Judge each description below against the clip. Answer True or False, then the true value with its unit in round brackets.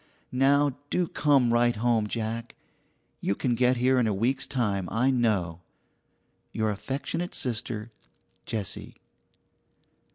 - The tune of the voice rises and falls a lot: False (3.1 semitones)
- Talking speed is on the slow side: True (120 wpm)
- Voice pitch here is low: True (120 Hz)